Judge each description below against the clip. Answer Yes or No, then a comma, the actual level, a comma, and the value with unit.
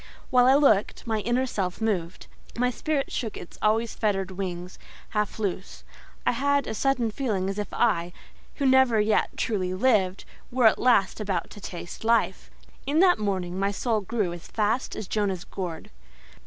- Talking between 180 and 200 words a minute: No, average, 170 wpm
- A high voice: Yes, high, 215 Hz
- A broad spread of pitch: No, average, 4.3 semitones